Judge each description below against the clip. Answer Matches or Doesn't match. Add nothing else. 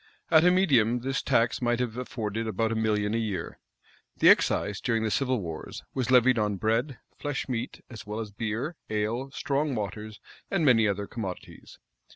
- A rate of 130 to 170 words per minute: Doesn't match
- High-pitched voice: Doesn't match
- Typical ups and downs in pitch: Matches